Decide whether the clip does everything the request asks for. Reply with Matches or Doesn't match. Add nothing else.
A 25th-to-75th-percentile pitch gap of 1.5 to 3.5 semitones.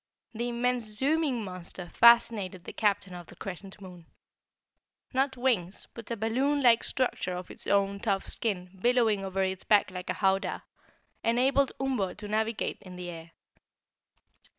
Doesn't match